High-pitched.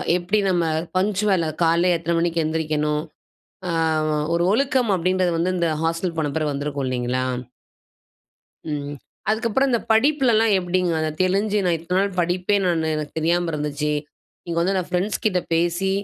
No: medium, 175 Hz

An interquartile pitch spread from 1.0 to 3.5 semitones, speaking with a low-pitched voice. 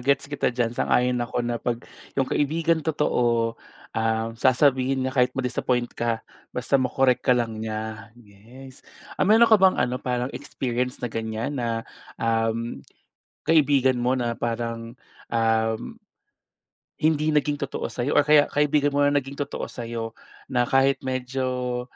Yes: average, 3.1 semitones; low, 125 Hz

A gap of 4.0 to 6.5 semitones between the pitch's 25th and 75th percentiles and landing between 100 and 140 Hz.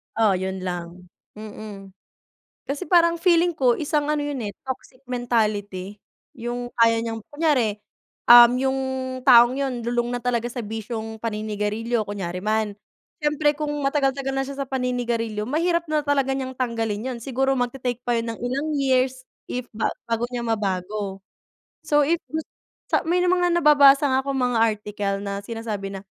No: average, 4.3 semitones; high, 240 Hz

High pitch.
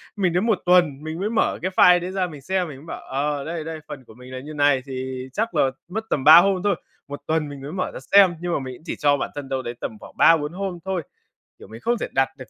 No: medium, 155 Hz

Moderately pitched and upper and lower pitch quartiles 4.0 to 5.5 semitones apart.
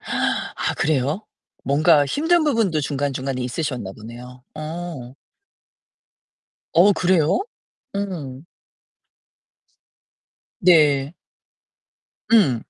Yes: medium, 150 Hz; average, 5.2 semitones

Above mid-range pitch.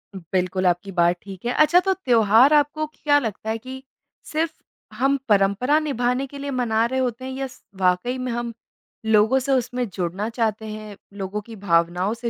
Yes: high, 235 Hz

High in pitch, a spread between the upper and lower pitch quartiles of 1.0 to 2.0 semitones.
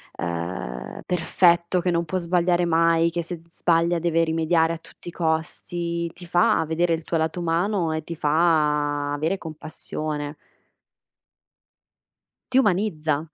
No: medium, 165 Hz; narrow, 1.7 semitones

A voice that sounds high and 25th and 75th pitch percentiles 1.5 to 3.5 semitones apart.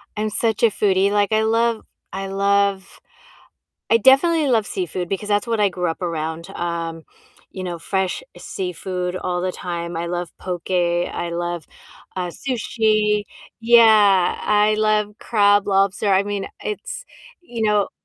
Yes: high, 200 Hz; average, 3.2 semitones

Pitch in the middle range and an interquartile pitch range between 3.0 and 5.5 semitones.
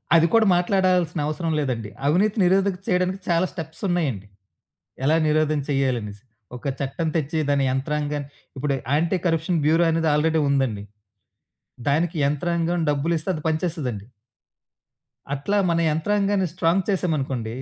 Yes: medium, 160 Hz; average, 3.9 semitones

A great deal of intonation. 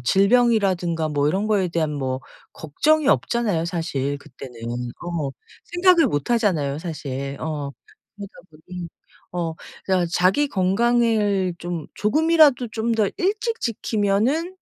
Yes: wide, 7.0 semitones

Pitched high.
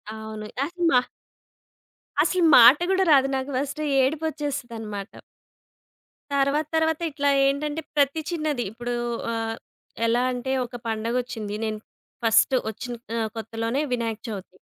Yes: very high, 250 Hz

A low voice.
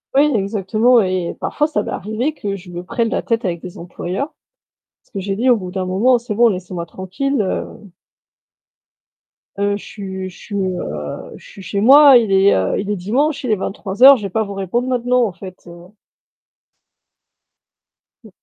No: high, 200 Hz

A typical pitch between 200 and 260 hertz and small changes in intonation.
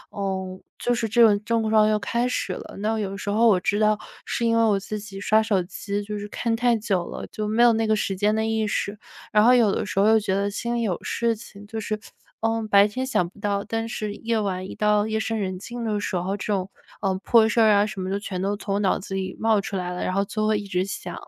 Yes: high, 210 Hz; narrow, 2.1 semitones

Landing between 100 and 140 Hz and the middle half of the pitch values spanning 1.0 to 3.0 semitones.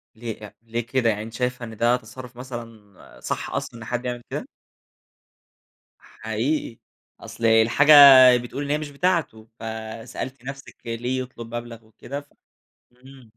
Yes: low, 120 Hz; narrow, 2.5 semitones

